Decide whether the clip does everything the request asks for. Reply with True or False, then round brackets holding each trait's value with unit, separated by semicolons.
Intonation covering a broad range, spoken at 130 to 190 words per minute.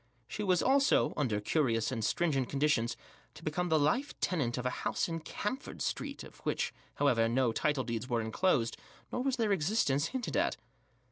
True (7.4 semitones; 180 wpm)